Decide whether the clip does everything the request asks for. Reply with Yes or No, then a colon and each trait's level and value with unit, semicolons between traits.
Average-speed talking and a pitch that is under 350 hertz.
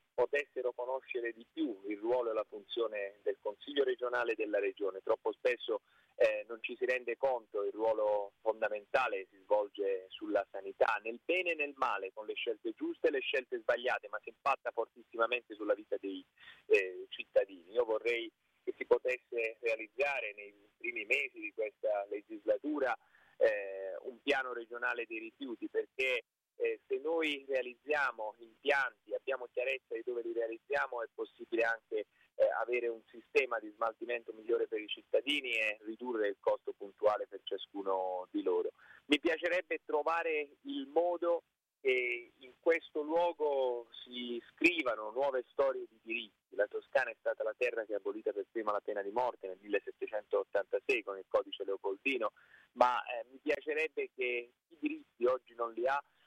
No: average, 160 wpm; very high, 390 Hz